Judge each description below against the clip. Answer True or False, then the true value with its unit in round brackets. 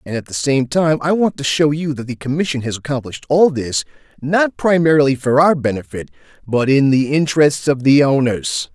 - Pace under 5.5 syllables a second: True (5.3 syllables/s)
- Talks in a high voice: False (140 Hz)